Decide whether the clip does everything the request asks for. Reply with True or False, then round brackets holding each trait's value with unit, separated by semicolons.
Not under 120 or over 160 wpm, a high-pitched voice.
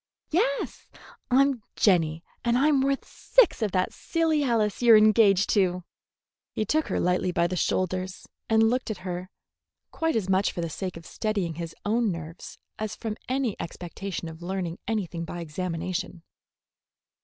True (155 wpm; 195 Hz)